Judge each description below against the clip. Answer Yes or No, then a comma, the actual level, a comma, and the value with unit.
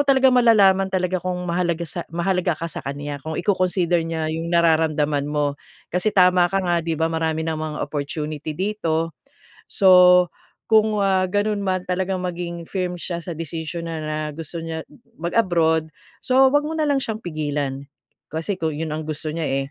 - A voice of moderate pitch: Yes, medium, 170 Hz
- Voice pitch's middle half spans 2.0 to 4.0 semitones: Yes, average, 2.9 semitones